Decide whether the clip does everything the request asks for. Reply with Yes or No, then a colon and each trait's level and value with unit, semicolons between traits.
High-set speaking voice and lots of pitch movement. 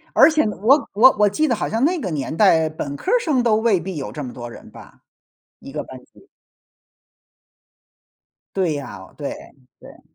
Yes: high, 195 Hz; wide, 8.7 semitones